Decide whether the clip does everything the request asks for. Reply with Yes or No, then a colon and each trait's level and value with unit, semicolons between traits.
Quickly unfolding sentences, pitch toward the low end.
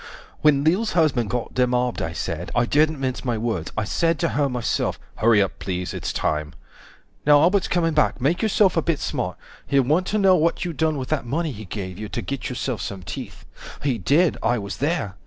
Yes: fast, 215 wpm; low, 130 Hz